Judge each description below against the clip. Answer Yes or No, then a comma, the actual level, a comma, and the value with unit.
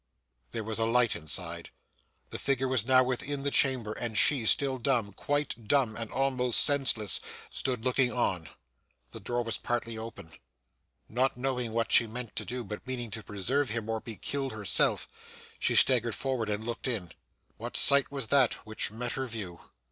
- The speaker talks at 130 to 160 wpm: No, average, 180 wpm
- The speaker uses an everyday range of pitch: Yes, average, 3.0 semitones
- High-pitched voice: No, low, 120 Hz